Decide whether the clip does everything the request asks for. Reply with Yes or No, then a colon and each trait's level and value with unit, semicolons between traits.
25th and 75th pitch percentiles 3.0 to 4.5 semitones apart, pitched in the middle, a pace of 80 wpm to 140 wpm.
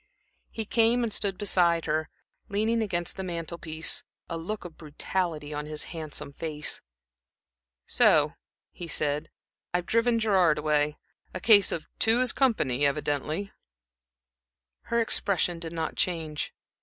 No: average, 5.0 semitones; medium, 170 Hz; slow, 135 wpm